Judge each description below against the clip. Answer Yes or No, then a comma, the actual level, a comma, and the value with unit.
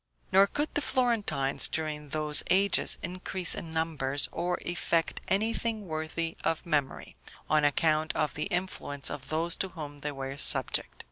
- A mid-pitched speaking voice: Yes, medium, 160 Hz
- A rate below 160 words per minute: Yes, average, 150 wpm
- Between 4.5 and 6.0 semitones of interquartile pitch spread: No, average, 3.7 semitones